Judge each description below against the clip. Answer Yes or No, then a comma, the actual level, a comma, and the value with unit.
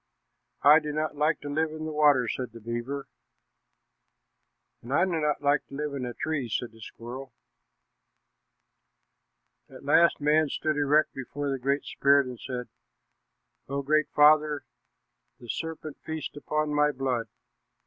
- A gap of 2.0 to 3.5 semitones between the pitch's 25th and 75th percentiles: Yes, narrow, 2.6 semitones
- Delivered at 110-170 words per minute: Yes, average, 150 wpm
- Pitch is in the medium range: Yes, medium, 145 Hz